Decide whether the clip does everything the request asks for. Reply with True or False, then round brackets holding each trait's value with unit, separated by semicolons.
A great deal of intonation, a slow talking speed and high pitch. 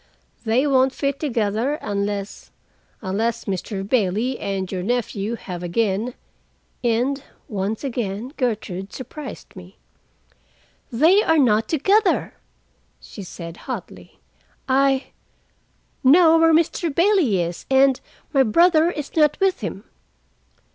True (6.4 semitones; 105 wpm; 245 Hz)